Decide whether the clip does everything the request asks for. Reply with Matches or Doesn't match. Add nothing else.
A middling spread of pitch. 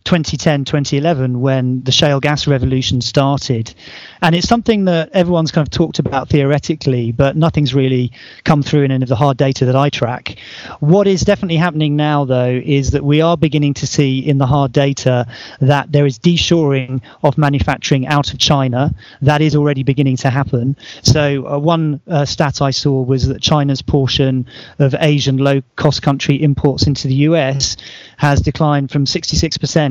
Doesn't match